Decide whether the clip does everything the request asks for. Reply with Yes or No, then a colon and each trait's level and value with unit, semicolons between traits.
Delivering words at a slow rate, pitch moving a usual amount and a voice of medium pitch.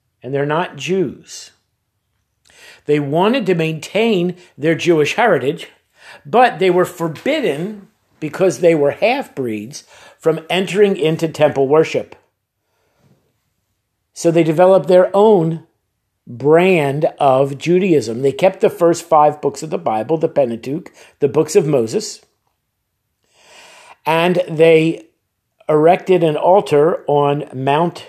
Yes: slow, 120 wpm; average, 4.1 semitones; medium, 160 Hz